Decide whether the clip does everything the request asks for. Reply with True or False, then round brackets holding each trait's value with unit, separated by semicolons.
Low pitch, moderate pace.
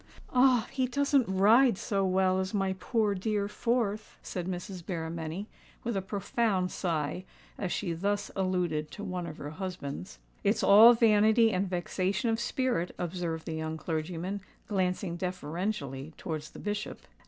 False (190 Hz; 150 wpm)